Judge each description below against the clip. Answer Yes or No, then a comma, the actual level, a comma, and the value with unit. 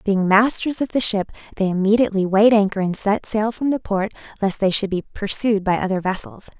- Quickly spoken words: Yes, fast, 210 wpm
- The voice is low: No, high, 205 Hz